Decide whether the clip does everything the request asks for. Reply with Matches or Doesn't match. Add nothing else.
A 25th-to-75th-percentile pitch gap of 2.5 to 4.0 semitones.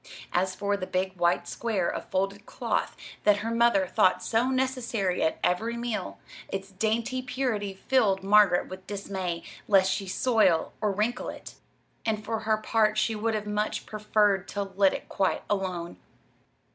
Matches